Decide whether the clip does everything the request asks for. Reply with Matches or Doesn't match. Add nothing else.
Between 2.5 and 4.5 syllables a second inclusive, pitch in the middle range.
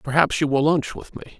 Doesn't match